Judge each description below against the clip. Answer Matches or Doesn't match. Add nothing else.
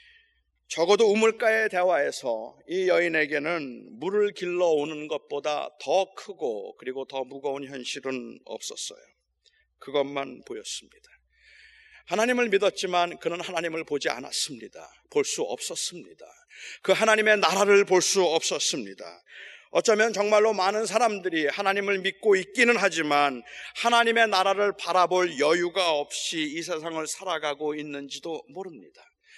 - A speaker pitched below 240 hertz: Matches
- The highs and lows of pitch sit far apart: Matches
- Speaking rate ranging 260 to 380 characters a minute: Matches